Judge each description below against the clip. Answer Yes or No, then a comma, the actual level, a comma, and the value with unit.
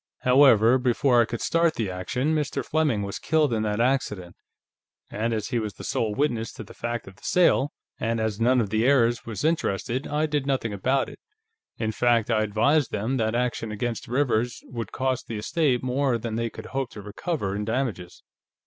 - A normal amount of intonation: Yes, average, 3.6 semitones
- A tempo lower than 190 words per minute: No, average, 195 wpm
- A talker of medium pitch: No, low, 120 Hz